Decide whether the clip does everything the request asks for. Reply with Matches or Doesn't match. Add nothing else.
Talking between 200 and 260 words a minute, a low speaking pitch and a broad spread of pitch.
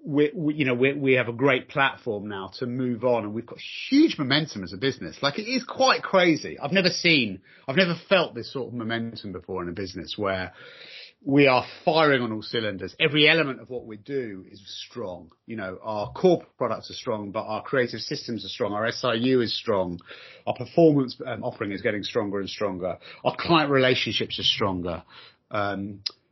Matches